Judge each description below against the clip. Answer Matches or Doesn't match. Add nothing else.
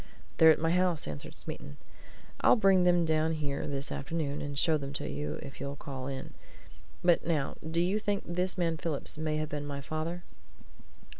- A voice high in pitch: Doesn't match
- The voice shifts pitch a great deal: Doesn't match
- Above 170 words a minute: Matches